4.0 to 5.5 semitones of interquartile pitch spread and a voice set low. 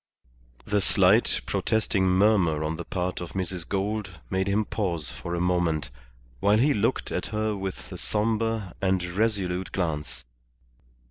No: average, 3.2 semitones; very low, 95 Hz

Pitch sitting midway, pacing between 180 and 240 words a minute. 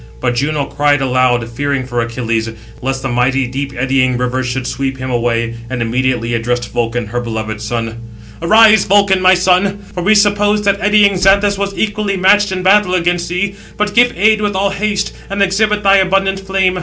Yes: medium, 175 Hz; average, 185 wpm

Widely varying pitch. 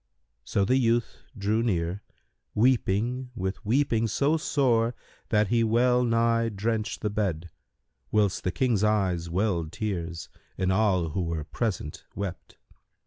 No: average, 3.8 semitones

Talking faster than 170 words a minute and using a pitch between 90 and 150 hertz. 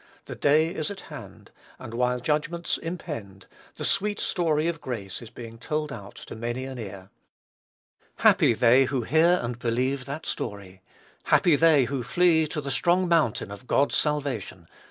No: average, 165 wpm; low, 135 Hz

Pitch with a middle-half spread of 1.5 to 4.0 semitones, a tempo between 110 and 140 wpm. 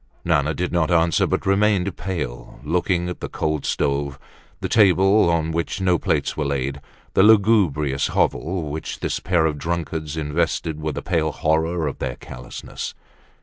No: average, 3.1 semitones; average, 160 wpm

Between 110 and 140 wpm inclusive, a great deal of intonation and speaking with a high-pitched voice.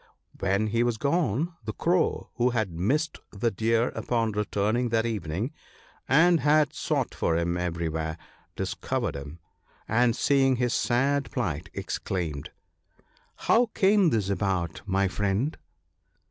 No: slow, 135 wpm; wide, 6.1 semitones; low, 110 Hz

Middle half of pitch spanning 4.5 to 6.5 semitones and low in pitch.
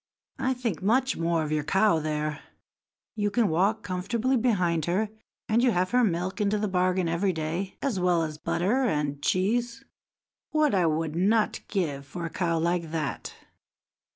No: average, 4.9 semitones; medium, 185 Hz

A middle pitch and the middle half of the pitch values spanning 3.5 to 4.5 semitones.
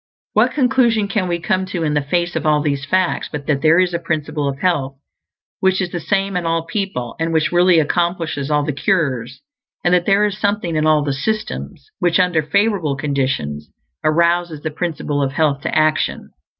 Yes: medium, 165 Hz; average, 3.9 semitones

